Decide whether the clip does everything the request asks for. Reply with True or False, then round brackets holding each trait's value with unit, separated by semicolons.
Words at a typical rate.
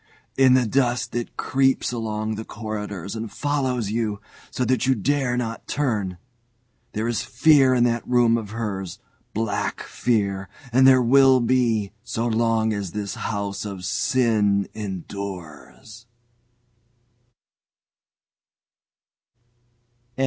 False (115 wpm)